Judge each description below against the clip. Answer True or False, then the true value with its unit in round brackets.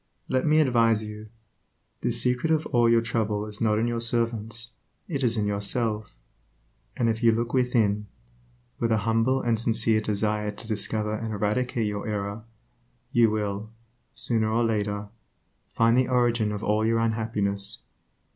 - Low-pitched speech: True (110 Hz)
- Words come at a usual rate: True (155 wpm)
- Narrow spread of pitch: True (1.8 semitones)